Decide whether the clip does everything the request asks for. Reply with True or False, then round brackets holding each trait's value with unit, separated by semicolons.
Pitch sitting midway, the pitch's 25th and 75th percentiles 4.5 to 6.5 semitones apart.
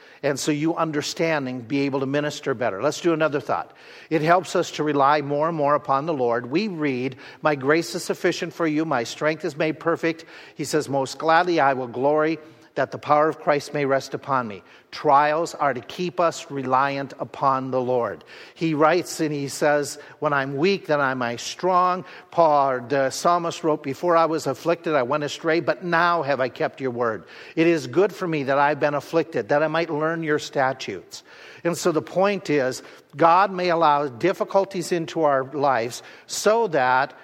False (150 Hz; 3.2 semitones)